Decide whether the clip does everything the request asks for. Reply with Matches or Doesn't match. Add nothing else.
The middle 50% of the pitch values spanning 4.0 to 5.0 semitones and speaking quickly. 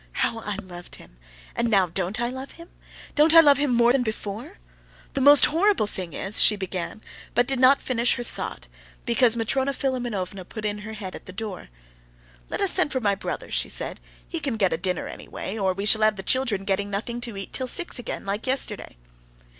Matches